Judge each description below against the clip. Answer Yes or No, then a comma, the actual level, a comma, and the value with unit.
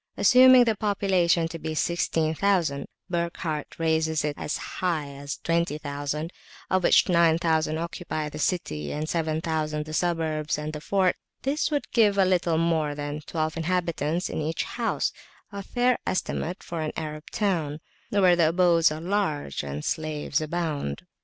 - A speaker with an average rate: Yes, average, 150 wpm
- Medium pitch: Yes, medium, 160 Hz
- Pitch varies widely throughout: No, average, 2.7 semitones